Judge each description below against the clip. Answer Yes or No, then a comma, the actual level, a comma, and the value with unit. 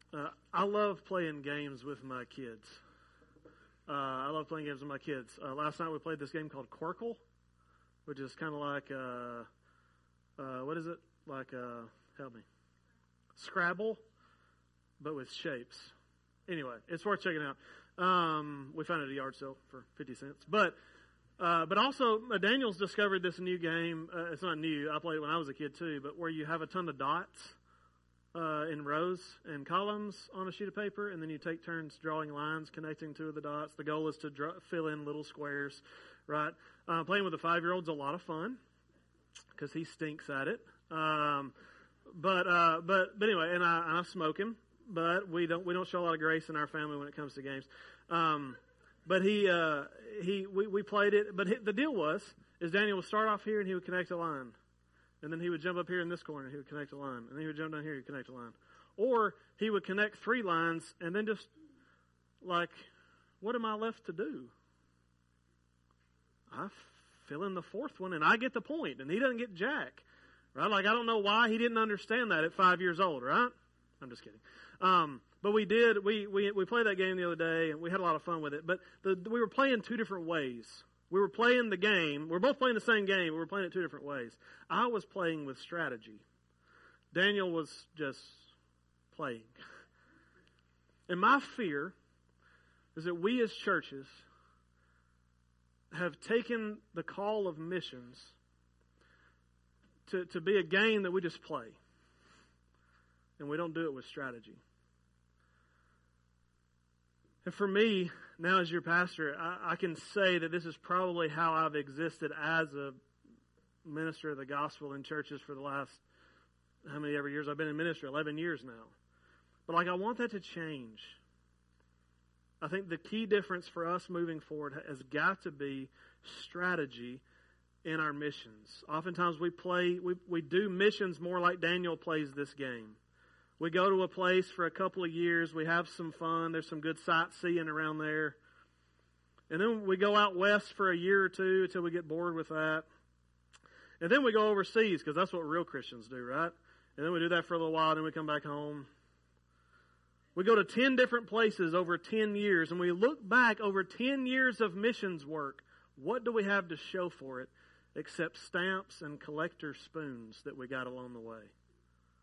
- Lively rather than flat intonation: Yes, wide, 6.4 semitones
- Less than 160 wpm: No, average, 195 wpm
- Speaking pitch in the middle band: Yes, medium, 160 Hz